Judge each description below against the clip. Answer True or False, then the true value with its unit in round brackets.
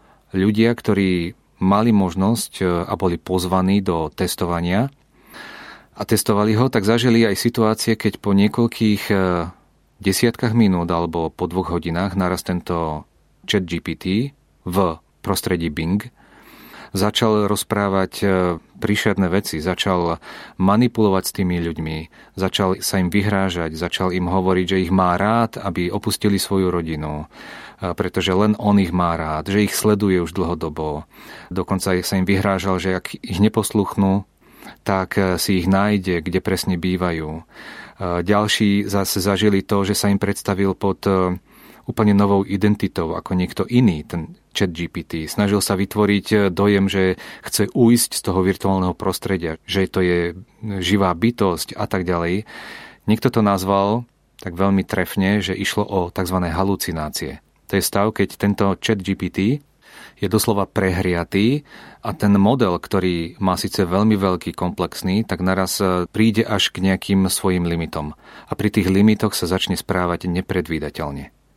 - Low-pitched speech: True (95 Hz)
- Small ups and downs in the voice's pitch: True (2.3 semitones)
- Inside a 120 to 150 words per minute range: True (140 wpm)